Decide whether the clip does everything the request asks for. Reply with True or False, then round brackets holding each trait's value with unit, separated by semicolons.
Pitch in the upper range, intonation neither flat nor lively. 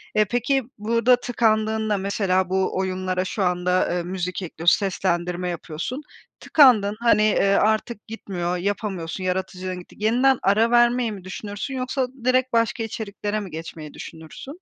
True (205 Hz; 4.0 semitones)